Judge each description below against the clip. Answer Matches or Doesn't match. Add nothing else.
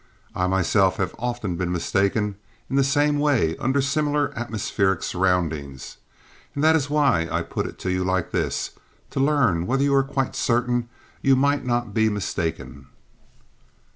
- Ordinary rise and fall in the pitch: Doesn't match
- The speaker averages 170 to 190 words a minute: Doesn't match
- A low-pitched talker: Matches